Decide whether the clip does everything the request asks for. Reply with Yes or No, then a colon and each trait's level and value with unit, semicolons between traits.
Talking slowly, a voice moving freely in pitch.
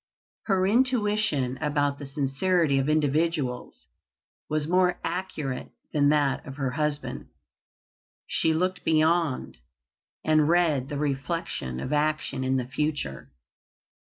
No: slow, 115 wpm; average, 3.7 semitones